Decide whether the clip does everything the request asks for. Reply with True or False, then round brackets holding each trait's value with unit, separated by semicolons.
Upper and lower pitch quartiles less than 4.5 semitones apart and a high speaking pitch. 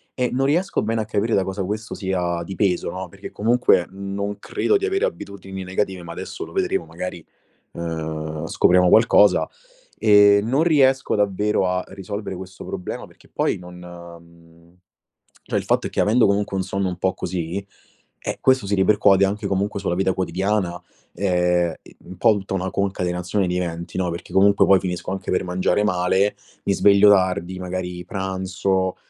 False (2.4 semitones; 95 Hz)